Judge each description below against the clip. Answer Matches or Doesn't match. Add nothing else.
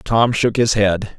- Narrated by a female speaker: Doesn't match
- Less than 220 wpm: Matches